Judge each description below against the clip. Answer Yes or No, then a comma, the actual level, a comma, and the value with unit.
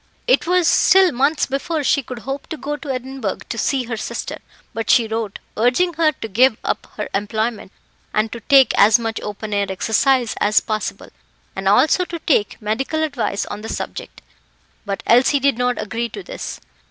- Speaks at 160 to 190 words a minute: Yes, average, 185 wpm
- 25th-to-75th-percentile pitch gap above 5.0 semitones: No, average, 4.6 semitones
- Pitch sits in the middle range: No, high, 245 Hz